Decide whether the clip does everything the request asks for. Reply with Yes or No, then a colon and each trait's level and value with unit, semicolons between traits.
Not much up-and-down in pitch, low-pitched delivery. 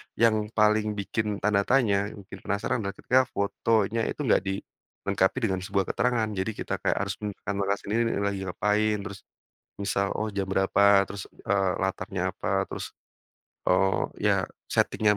Yes: narrow, 1.7 semitones; low, 100 Hz